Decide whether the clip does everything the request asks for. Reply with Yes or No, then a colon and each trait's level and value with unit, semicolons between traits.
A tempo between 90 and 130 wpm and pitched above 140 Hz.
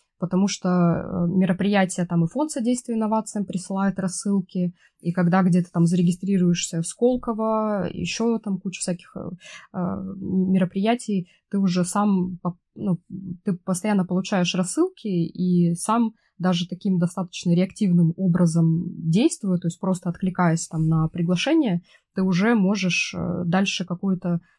Yes: average, 125 wpm; medium, 185 Hz